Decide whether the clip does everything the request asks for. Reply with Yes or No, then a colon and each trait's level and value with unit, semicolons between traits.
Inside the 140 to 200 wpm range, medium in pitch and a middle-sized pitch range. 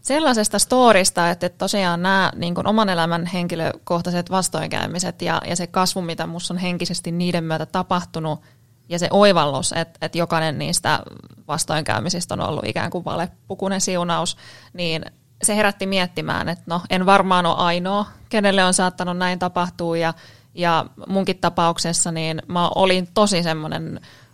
No: average, 150 wpm; medium, 175 Hz; narrow, 2.2 semitones